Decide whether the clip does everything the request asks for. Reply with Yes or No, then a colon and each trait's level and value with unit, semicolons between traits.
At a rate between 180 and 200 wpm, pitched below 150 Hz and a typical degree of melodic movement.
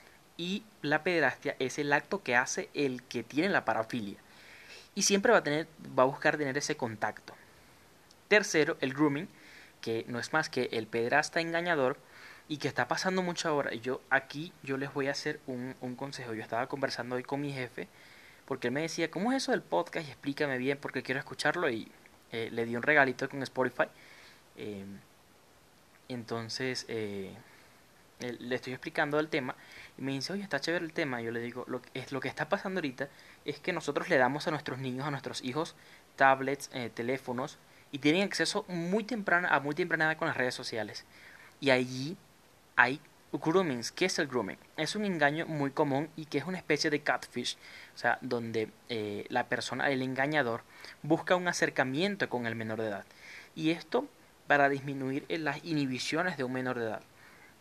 Yes: fast, 190 wpm; medium, 140 Hz; average, 3.9 semitones